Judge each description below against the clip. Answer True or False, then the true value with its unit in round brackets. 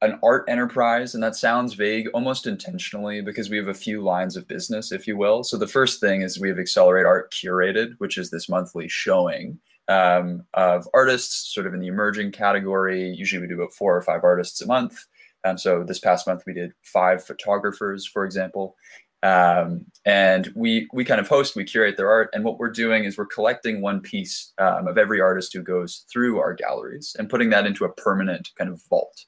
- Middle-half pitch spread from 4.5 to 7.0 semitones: False (3.8 semitones)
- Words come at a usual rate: False (215 wpm)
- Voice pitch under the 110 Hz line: True (100 Hz)